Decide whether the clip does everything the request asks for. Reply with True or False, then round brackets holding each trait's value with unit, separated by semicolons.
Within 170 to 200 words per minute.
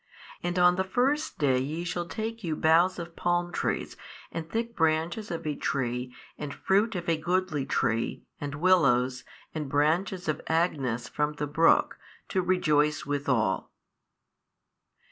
False (145 wpm)